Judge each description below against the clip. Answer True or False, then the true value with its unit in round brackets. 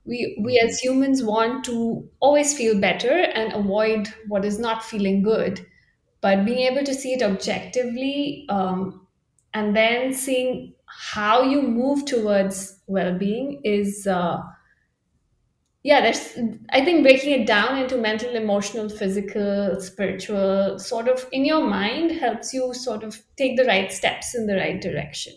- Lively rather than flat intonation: False (4.2 semitones)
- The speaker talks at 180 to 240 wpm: False (150 wpm)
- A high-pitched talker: True (225 Hz)